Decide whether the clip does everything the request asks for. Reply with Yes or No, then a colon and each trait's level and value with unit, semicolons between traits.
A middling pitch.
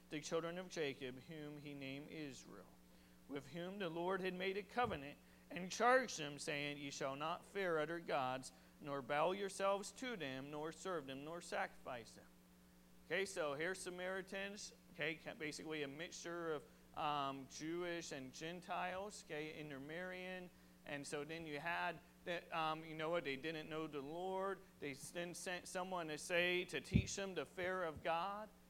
Yes: medium, 160 Hz